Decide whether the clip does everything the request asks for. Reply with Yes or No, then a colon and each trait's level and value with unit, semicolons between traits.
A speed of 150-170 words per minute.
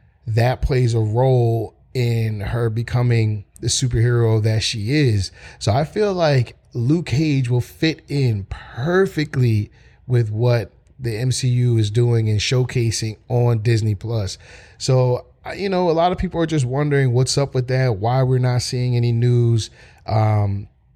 Yes: average, 160 wpm